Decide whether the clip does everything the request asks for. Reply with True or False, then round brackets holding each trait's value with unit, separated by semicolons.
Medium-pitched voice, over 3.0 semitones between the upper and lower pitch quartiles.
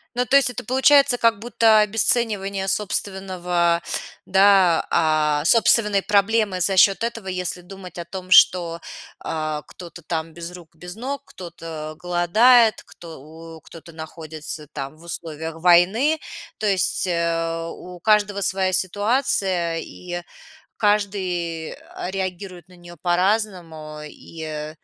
True (180 Hz; 3.6 semitones)